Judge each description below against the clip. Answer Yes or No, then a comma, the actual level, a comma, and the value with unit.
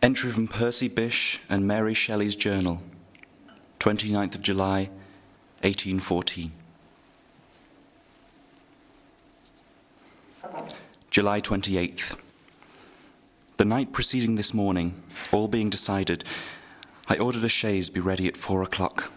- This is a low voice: Yes, low, 100 Hz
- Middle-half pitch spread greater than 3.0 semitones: No, average, 2.7 semitones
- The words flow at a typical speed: No, slow, 95 wpm